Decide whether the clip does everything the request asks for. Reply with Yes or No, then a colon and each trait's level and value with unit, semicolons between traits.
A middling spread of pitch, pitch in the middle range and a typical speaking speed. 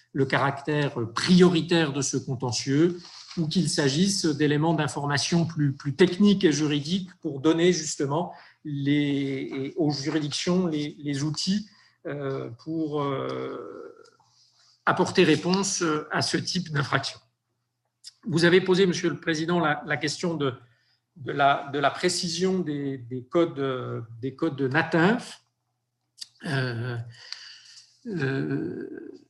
No: average, 4.4 semitones; medium, 150 Hz; slow, 115 wpm